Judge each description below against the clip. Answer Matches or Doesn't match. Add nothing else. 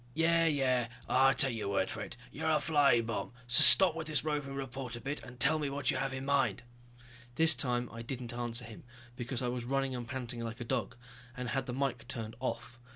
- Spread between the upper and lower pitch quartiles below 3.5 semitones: Matches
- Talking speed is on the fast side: Matches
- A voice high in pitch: Doesn't match